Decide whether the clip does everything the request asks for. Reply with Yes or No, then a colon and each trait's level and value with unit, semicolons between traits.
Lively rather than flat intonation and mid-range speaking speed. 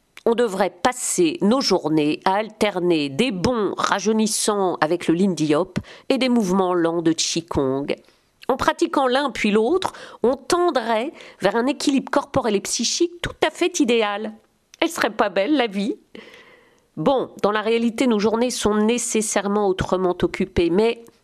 Yes: wide, 6.3 semitones; average, 155 wpm